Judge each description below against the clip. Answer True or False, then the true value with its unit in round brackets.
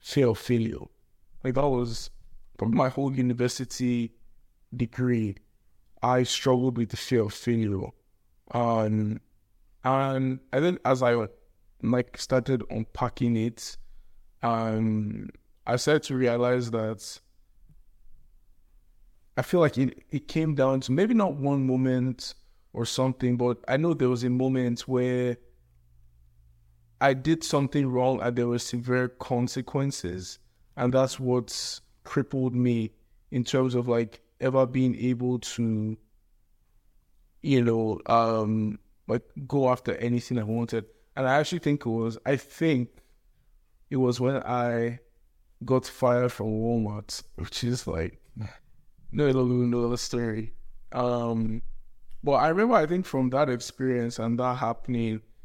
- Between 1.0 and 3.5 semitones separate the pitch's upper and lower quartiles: True (2.6 semitones)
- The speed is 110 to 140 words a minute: True (135 wpm)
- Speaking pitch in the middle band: False (120 Hz)